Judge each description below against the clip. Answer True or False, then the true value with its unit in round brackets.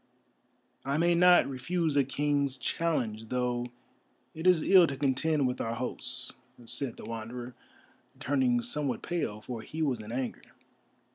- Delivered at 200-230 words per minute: False (145 wpm)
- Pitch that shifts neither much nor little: True (4.0 semitones)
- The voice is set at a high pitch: False (130 Hz)